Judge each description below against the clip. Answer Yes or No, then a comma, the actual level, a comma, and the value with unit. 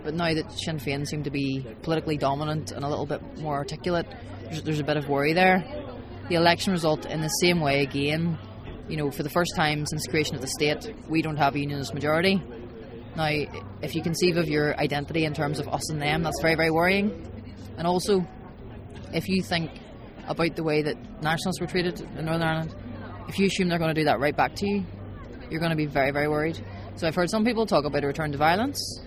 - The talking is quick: Yes, fast, 225 wpm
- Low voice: No, medium, 150 Hz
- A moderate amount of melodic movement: Yes, average, 3.1 semitones